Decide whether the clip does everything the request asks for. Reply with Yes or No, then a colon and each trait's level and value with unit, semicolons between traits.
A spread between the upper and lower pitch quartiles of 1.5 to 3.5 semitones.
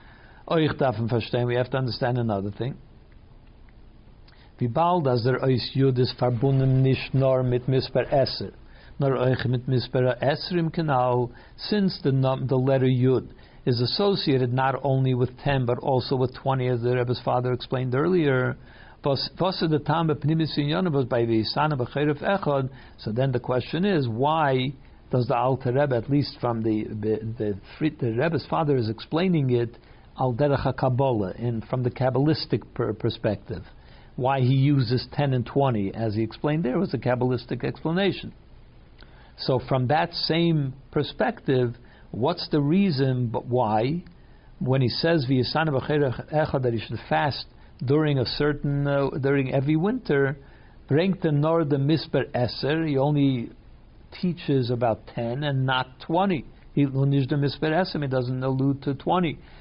Yes: average, 3.1 semitones